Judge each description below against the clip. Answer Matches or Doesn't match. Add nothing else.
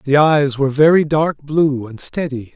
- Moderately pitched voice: Matches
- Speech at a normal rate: Matches